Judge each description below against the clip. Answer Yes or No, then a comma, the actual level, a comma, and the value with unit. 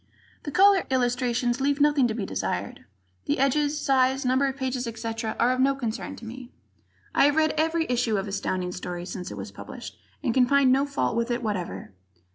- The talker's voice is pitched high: Yes, very high, 255 Hz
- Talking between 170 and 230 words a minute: Yes, average, 200 wpm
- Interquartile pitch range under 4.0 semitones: Yes, average, 3.6 semitones